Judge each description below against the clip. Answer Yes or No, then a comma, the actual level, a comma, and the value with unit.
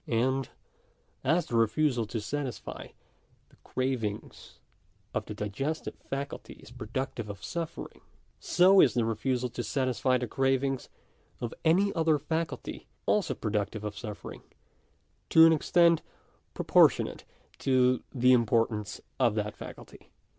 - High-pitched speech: No, low, 130 Hz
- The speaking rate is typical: No, slow, 125 wpm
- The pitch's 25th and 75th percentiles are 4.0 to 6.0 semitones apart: Yes, average, 4.6 semitones